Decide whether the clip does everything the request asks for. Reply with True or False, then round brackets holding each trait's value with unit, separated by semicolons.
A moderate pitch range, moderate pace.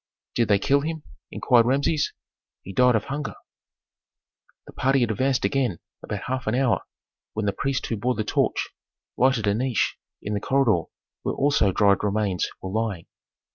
True (4.7 semitones; 170 wpm)